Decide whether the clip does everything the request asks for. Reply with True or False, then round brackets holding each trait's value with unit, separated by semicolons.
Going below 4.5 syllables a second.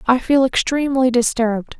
False (5.5 syllables/s)